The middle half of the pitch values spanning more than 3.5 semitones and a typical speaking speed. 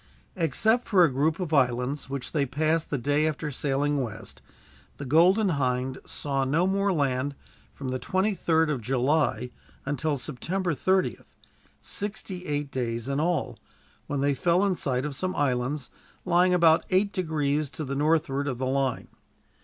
Yes: average, 4.2 semitones; average, 160 wpm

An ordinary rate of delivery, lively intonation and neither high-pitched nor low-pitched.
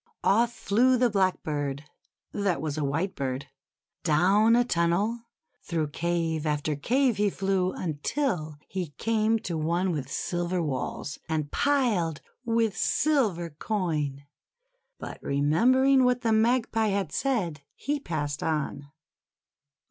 No: slow, 120 wpm; wide, 6.9 semitones; medium, 180 Hz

